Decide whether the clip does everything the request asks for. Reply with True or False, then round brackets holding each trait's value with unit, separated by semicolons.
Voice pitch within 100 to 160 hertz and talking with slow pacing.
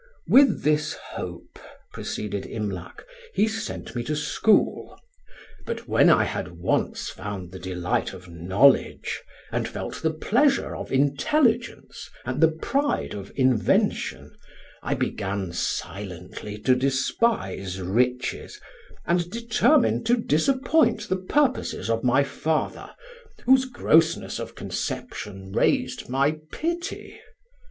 True (140 Hz; 115 wpm)